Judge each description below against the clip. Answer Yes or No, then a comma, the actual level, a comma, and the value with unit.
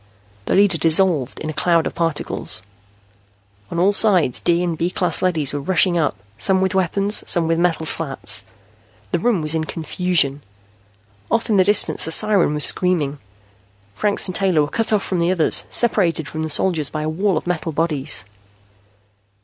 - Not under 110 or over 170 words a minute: No, average, 180 wpm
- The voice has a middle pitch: Yes, medium, 170 Hz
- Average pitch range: Yes, average, 3.3 semitones